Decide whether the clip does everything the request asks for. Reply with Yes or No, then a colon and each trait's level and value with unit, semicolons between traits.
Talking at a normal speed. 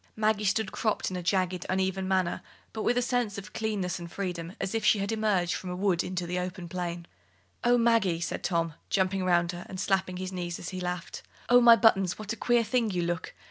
No: fast, 225 wpm